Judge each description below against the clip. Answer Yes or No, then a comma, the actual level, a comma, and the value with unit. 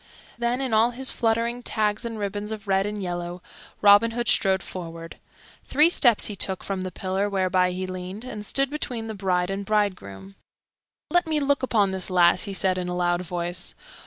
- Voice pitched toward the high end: Yes, high, 200 Hz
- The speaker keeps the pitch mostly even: No, average, 3.9 semitones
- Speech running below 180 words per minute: No, average, 190 wpm